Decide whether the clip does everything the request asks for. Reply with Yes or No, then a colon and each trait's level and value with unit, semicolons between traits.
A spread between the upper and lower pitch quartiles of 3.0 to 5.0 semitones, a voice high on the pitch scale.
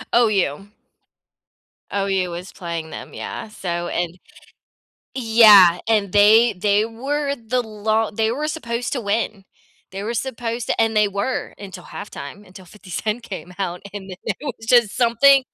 Yes: average, 3.4 semitones; high, 210 Hz